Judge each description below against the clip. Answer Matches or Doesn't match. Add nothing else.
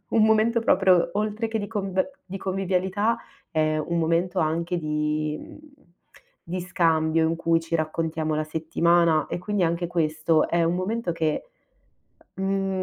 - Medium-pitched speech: Matches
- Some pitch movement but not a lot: Matches